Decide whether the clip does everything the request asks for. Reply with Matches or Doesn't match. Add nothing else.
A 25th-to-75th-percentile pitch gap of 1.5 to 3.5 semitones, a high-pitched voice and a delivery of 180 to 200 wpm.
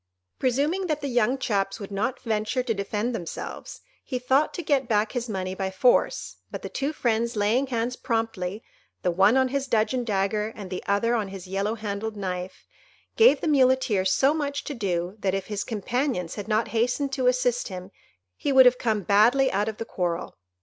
Doesn't match